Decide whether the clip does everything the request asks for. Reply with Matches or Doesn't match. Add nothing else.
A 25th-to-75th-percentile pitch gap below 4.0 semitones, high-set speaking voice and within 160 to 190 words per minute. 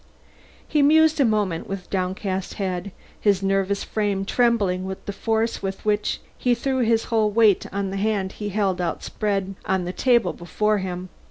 Matches